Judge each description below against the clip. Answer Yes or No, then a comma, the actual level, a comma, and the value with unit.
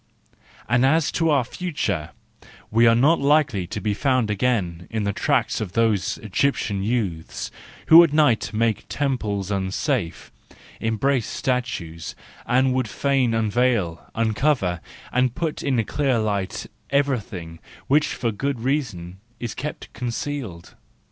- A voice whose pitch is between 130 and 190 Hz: No, low, 115 Hz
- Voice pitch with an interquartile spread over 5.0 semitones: Yes, wide, 5.4 semitones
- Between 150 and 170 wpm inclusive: No, slow, 135 wpm